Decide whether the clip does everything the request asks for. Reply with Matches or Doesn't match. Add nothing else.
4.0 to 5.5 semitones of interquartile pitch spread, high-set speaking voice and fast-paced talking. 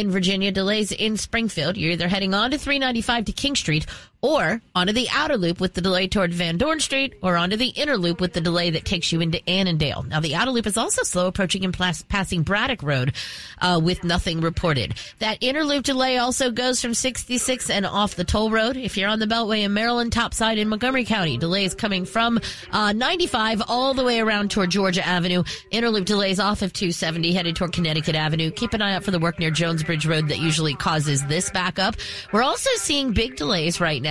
Matches